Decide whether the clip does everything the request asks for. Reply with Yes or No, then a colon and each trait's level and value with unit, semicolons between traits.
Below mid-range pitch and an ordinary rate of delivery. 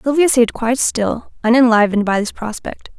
No: high, 235 Hz; average, 160 wpm